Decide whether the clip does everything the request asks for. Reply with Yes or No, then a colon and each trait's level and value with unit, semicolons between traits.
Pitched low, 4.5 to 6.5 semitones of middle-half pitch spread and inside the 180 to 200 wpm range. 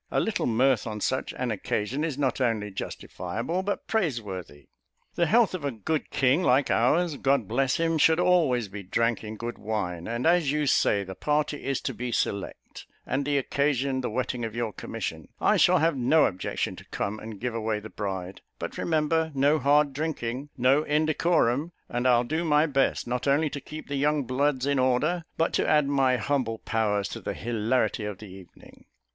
Yes: low, 130 Hz; average, 5.0 semitones; average, 195 wpm